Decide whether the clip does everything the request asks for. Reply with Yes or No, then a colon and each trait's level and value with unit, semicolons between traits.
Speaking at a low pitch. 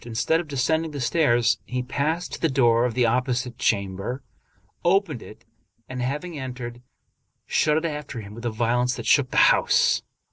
Yes: low, 125 Hz